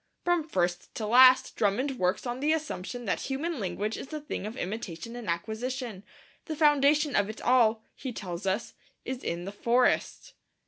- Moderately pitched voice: No, high, 240 Hz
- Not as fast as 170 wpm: No, average, 175 wpm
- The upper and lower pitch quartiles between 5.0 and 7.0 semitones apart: Yes, wide, 5.4 semitones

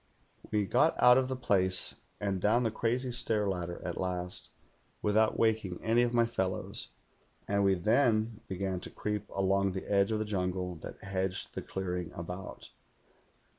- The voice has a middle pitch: No, low, 100 Hz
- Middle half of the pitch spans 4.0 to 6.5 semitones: No, average, 3.3 semitones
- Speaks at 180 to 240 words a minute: No, average, 165 wpm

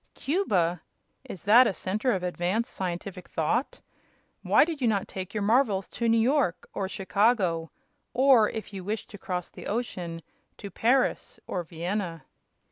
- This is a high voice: Yes, high, 200 Hz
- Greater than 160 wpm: No, average, 155 wpm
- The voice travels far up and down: No, average, 4.6 semitones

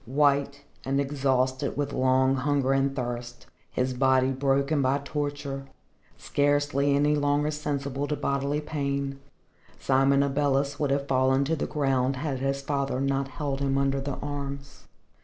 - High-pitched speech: No, medium, 140 Hz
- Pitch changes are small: Yes, narrow, 1.1 semitones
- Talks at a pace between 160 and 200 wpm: No, average, 145 wpm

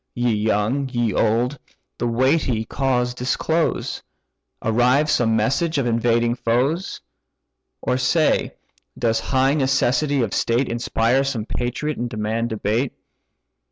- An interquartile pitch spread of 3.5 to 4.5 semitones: No, average, 2.9 semitones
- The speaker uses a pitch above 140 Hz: No, low, 125 Hz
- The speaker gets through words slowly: Yes, slow, 120 wpm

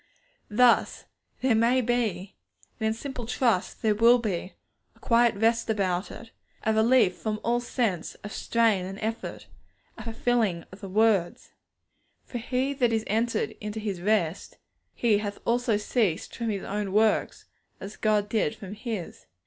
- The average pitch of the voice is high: Yes, high, 220 Hz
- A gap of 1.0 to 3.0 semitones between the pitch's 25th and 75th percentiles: Yes, narrow, 2.6 semitones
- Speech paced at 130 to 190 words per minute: Yes, average, 155 wpm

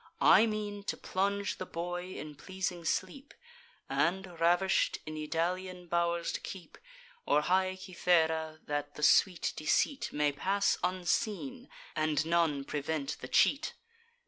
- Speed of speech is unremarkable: No, slow, 130 wpm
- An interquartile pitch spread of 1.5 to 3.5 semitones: Yes, average, 3.2 semitones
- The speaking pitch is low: No, medium, 175 Hz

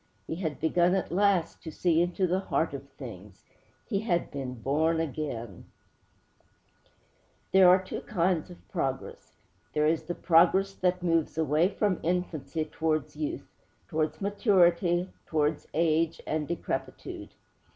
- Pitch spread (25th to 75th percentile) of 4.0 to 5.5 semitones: No, average, 2.8 semitones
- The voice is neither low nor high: Yes, medium, 170 Hz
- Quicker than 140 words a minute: No, slow, 135 wpm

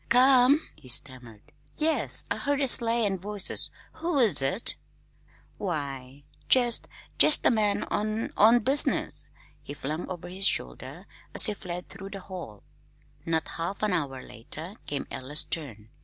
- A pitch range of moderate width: No, wide, 8.1 semitones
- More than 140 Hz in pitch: Yes, high, 190 Hz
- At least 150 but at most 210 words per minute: Yes, average, 155 wpm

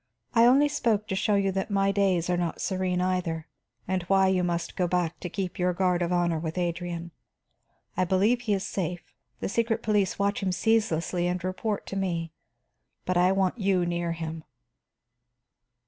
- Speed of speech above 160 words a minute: Yes, average, 180 wpm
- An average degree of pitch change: No, narrow, 2.3 semitones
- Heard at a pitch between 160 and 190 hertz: Yes, medium, 185 Hz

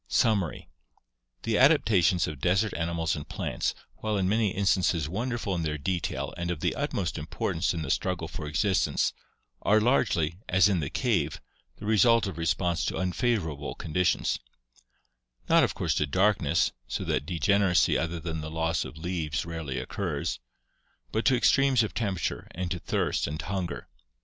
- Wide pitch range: No, average, 4.1 semitones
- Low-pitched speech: Yes, very low, 90 Hz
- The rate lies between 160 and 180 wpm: Yes, average, 165 wpm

